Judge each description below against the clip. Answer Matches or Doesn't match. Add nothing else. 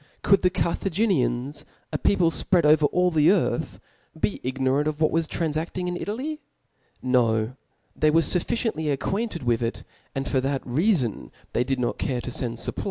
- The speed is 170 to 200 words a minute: Matches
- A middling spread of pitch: Doesn't match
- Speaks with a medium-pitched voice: Matches